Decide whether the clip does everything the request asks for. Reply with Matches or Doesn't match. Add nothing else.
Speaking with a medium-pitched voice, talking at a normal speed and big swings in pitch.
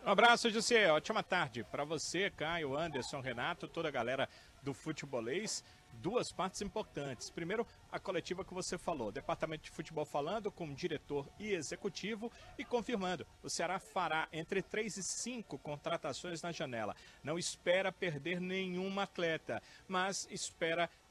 Doesn't match